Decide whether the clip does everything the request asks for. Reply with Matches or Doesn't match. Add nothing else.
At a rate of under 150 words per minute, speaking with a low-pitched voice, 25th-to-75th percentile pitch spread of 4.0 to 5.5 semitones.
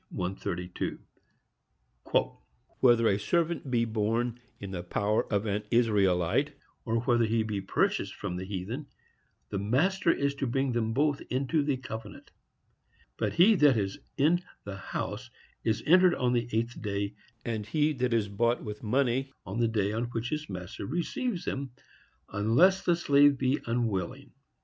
Doesn't match